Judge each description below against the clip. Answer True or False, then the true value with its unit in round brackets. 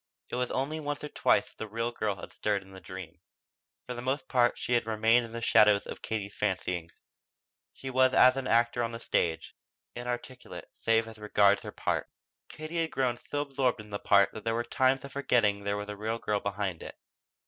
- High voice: False (115 Hz)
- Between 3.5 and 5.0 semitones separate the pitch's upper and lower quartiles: True (3.8 semitones)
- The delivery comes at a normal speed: False (215 wpm)